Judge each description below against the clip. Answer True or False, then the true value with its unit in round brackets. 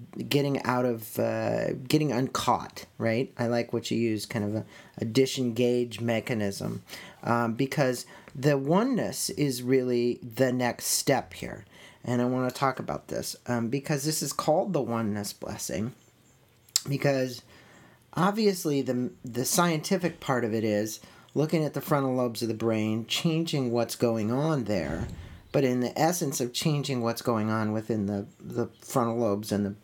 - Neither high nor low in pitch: False (125 Hz)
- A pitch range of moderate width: True (3.8 semitones)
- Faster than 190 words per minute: False (165 wpm)